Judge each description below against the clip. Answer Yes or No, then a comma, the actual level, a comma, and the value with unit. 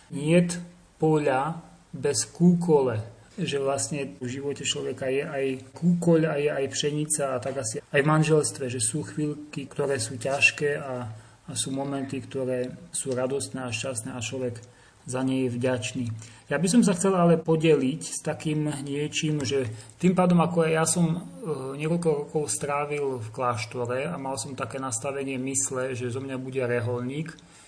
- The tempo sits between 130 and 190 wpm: Yes, fast, 165 wpm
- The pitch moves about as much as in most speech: Yes, average, 3.0 semitones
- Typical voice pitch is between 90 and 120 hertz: No, medium, 140 Hz